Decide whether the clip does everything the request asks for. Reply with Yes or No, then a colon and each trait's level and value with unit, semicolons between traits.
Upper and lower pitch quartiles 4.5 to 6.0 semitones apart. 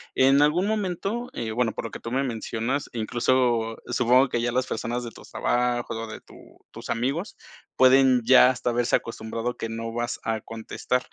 No: narrow, 2.5 semitones